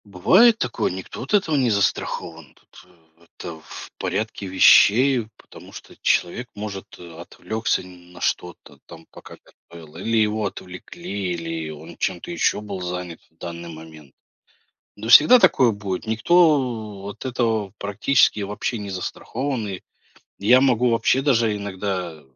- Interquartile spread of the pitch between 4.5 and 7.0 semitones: Yes, average, 5.1 semitones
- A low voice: Yes, low, 100 Hz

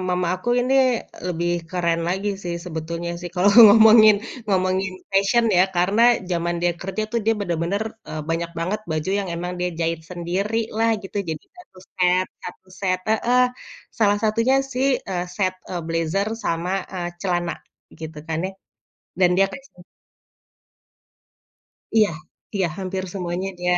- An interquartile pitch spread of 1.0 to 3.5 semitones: Yes, average, 2.8 semitones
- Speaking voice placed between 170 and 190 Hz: Yes, medium, 185 Hz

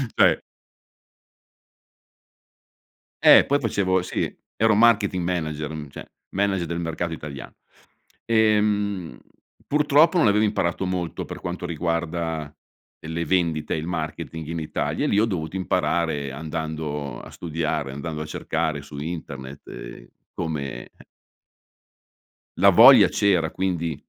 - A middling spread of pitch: Yes, average, 3.7 semitones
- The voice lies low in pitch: Yes, very low, 85 Hz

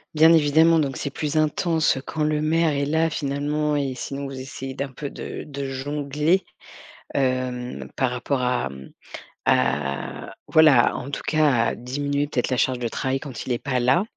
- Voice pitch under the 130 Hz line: No, medium, 140 Hz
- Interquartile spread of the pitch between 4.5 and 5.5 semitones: No, average, 2.9 semitones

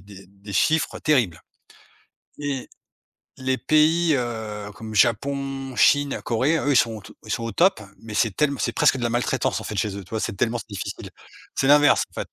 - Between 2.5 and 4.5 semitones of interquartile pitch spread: No, average, 5.0 semitones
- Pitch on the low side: Yes, low, 120 Hz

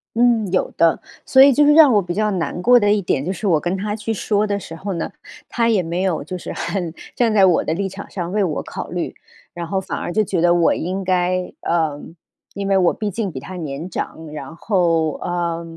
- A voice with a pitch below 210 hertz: Yes, medium, 185 Hz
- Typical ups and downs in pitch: Yes, average, 3.5 semitones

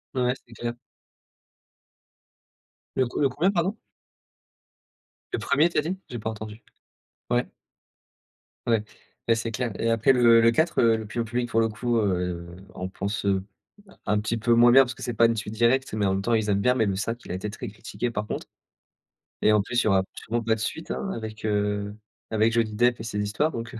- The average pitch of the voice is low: Yes, low, 115 Hz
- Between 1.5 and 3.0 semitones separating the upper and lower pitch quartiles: Yes, narrow, 2.4 semitones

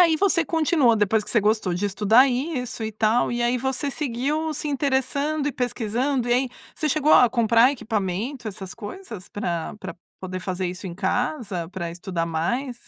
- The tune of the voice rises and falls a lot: Yes, wide, 5.7 semitones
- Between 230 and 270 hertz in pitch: Yes, high, 240 Hz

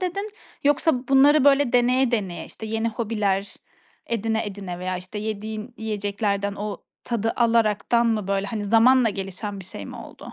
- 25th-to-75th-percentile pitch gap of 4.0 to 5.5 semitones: No, average, 3.1 semitones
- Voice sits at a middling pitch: No, high, 220 Hz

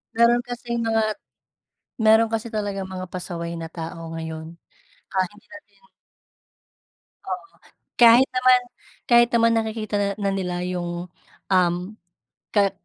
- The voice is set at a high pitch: Yes, high, 200 Hz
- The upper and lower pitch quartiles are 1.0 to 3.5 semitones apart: No, average, 4.8 semitones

